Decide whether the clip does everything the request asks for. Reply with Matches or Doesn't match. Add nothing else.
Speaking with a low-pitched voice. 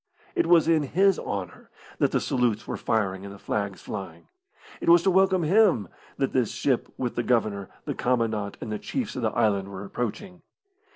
Matches